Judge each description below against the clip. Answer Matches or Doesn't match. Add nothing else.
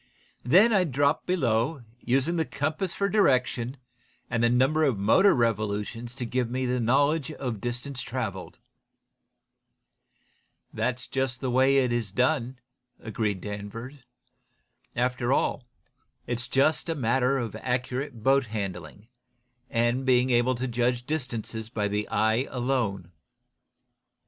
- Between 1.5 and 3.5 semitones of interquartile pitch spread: Matches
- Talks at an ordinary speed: Doesn't match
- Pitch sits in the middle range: Doesn't match